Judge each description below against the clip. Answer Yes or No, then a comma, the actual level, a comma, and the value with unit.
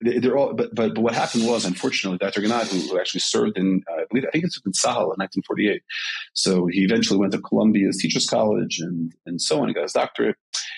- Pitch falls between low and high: No, very low, 95 Hz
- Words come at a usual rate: No, fast, 225 wpm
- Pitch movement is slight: No, average, 4.1 semitones